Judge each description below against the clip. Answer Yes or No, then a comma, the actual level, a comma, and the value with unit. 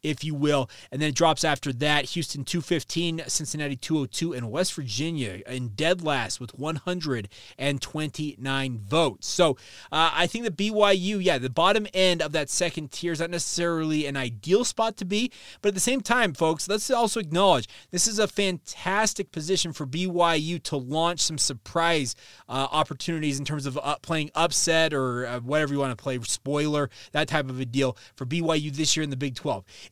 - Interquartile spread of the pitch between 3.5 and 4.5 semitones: Yes, average, 3.8 semitones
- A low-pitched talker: No, medium, 155 Hz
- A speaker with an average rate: Yes, average, 195 wpm